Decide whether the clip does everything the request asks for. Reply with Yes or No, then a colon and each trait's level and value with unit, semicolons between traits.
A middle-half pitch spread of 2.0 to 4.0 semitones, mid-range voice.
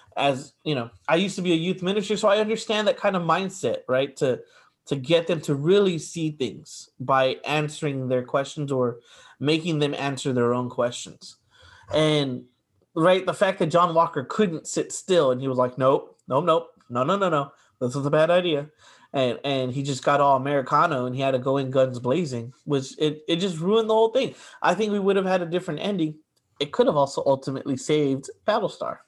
No: average, 4.9 semitones; medium, 145 Hz